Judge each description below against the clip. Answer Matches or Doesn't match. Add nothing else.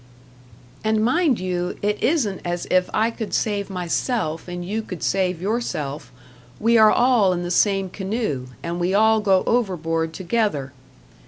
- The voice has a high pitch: Matches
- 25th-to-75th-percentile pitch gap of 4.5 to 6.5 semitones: Doesn't match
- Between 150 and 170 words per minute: Matches